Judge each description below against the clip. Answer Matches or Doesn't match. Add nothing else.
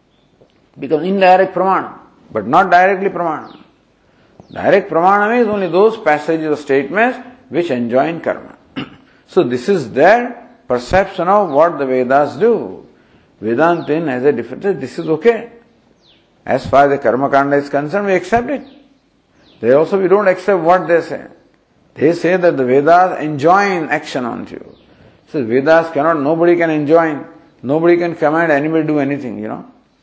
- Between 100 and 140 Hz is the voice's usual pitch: Doesn't match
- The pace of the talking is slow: Doesn't match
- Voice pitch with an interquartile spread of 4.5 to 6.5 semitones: Matches